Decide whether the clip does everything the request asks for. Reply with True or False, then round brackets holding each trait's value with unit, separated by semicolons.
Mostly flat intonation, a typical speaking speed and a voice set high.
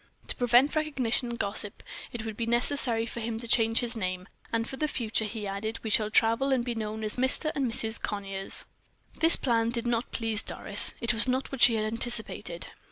False (2.0 semitones; 210 wpm; 230 Hz)